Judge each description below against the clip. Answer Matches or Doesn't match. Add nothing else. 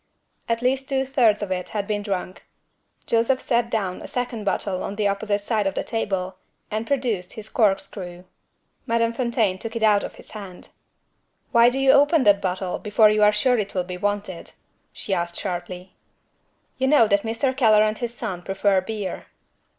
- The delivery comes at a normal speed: Matches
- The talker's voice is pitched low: Doesn't match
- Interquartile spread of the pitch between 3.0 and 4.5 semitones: Matches